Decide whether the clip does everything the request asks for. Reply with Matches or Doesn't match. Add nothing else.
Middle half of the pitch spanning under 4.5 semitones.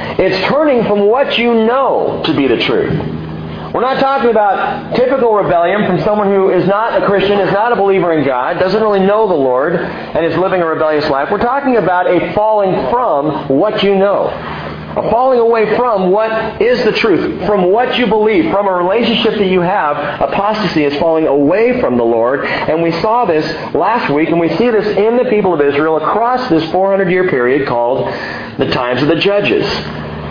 Doesn't match